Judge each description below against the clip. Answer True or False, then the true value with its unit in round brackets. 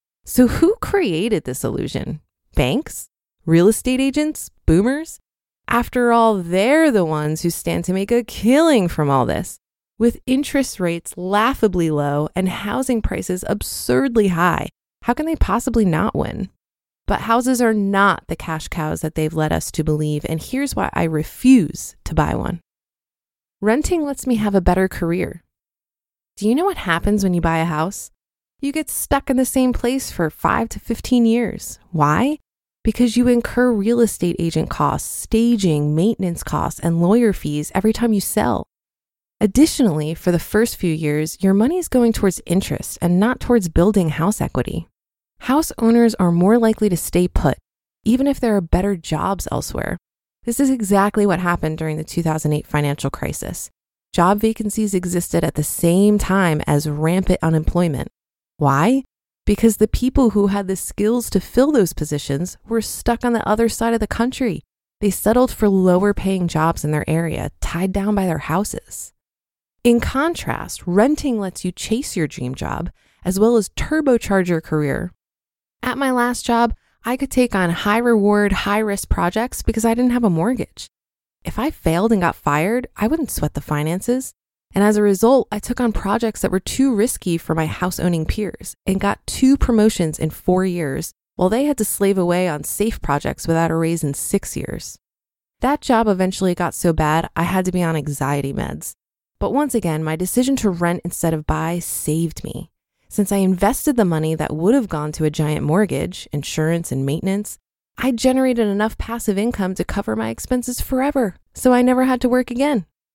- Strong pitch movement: True (6.1 semitones)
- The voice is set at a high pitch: True (200 Hz)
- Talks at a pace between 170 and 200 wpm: True (180 wpm)